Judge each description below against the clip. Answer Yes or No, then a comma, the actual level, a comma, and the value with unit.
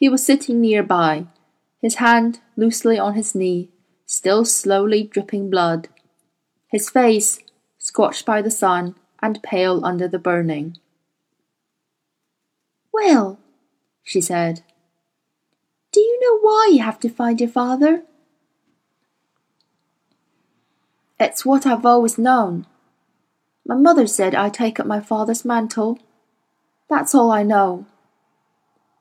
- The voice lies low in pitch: No, high, 215 Hz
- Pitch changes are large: No, average, 4.9 semitones